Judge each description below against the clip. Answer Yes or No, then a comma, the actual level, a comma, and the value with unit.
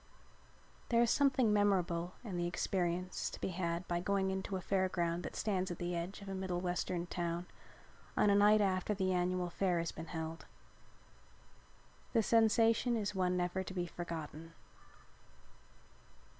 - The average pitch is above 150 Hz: Yes, medium, 185 Hz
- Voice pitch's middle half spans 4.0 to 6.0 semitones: No, narrow, 2.4 semitones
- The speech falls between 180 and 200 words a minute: No, average, 160 wpm